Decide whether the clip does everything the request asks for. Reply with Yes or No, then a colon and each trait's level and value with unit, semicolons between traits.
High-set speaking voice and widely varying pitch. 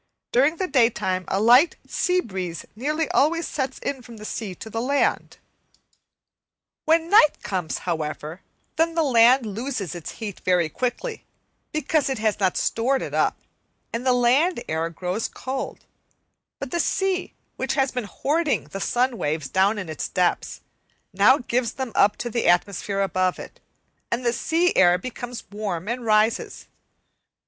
Yes: high, 235 Hz; wide, 6.1 semitones